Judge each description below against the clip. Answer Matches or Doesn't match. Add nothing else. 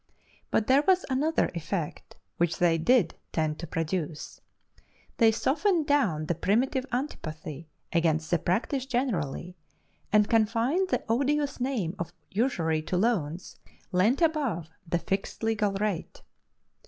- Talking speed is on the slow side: Matches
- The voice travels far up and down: Matches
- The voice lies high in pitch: Matches